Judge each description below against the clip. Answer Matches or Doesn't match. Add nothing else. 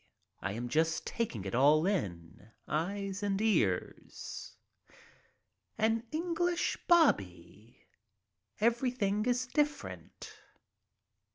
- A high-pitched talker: Matches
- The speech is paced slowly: Matches